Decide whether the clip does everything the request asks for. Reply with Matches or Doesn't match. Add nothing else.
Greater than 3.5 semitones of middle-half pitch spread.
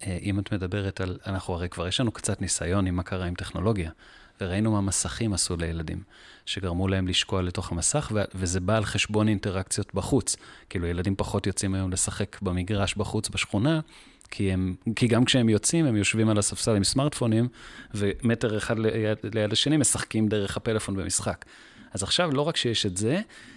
Doesn't match